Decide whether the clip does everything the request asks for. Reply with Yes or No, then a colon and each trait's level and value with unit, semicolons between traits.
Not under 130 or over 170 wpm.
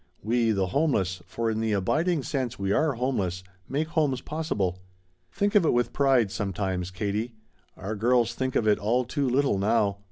No: average, 180 wpm